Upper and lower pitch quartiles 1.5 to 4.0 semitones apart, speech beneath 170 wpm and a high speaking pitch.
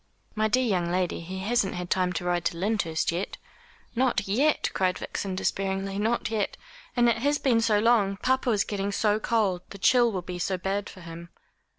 No: average, 3.7 semitones; average, 200 wpm; high, 200 Hz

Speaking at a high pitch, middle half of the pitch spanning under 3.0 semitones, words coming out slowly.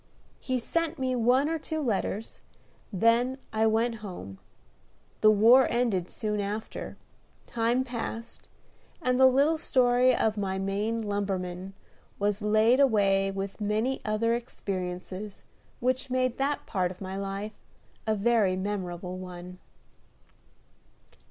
No: high, 215 Hz; average, 4.2 semitones; slow, 125 wpm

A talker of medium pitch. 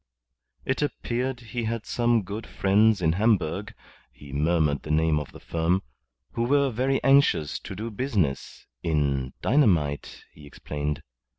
No: very low, 95 Hz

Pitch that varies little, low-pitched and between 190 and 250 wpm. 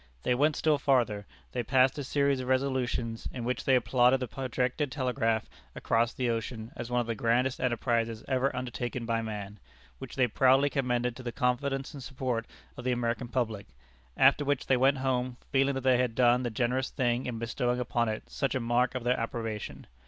Yes: narrow, 2.0 semitones; low, 125 Hz; average, 195 wpm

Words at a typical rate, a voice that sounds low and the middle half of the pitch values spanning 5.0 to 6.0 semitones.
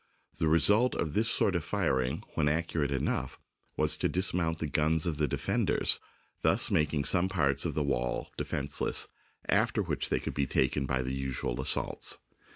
No: average, 170 wpm; very low, 75 Hz; average, 3.3 semitones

